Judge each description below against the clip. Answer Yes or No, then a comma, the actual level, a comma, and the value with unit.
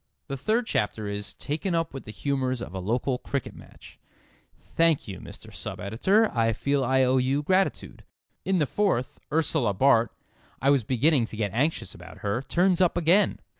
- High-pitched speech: No, low, 135 Hz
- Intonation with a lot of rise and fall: Yes, wide, 6.3 semitones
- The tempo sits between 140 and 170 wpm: No, average, 180 wpm